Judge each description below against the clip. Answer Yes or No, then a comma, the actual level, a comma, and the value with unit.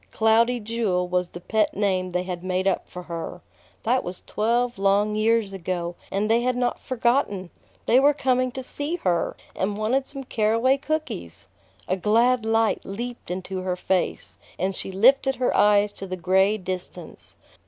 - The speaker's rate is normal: Yes, average, 170 wpm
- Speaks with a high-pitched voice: Yes, high, 210 Hz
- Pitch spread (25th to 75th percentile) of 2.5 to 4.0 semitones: No, average, 4.6 semitones